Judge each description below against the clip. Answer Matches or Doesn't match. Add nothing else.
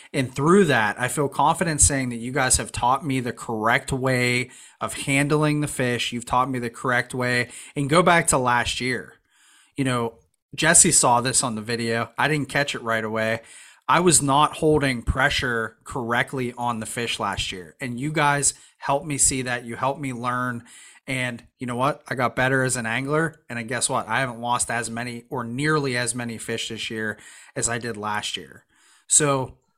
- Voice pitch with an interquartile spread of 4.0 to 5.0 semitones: Doesn't match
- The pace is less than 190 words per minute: Doesn't match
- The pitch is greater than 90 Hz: Matches